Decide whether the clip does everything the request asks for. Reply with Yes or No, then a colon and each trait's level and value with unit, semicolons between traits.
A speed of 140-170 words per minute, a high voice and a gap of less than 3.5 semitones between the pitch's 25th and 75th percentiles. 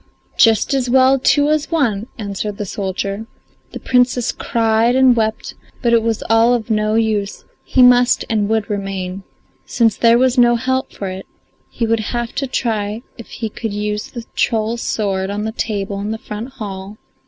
No: average, 180 wpm; high, 225 Hz; average, 2.8 semitones